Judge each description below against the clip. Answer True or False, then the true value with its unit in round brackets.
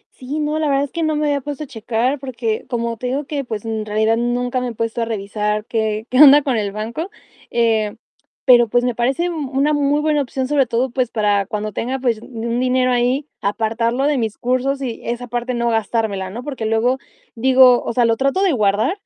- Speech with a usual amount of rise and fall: True (3.3 semitones)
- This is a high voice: True (245 Hz)